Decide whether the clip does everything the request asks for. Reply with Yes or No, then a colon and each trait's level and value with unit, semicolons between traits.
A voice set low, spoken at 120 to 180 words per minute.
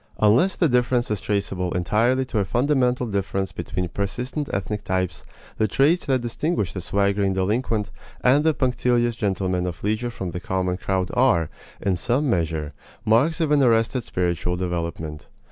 Yes: low, 105 Hz; average, 160 wpm